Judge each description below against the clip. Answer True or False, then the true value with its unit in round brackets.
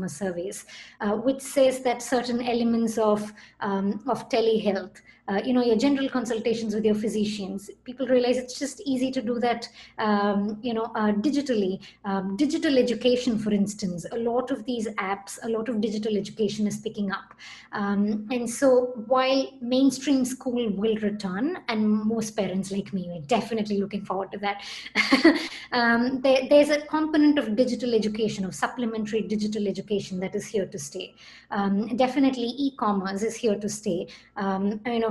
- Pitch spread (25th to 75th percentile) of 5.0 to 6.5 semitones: False (3.5 semitones)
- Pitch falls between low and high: False (225 Hz)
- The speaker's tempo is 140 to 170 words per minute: True (165 wpm)